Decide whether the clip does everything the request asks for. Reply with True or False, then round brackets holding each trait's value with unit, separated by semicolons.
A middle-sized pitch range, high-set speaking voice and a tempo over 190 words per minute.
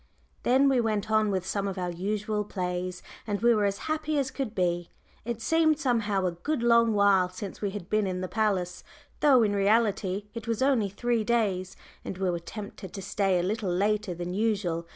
True (3.7 semitones; 205 Hz; 205 wpm)